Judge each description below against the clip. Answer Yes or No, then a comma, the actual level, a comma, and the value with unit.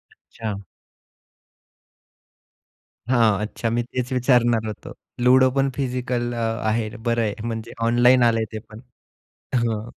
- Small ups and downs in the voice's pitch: Yes, narrow, 1.9 semitones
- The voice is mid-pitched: No, low, 120 Hz